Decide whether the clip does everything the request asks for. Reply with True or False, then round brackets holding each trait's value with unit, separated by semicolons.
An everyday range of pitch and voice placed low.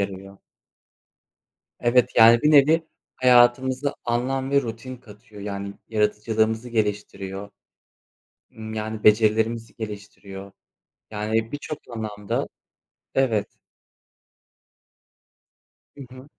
True (3.0 semitones; 110 Hz)